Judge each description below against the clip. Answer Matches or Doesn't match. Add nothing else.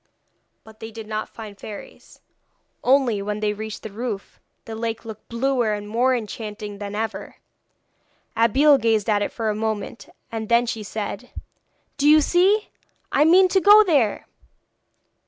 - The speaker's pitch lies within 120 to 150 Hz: Doesn't match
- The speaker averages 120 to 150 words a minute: Doesn't match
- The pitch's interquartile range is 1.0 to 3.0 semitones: Doesn't match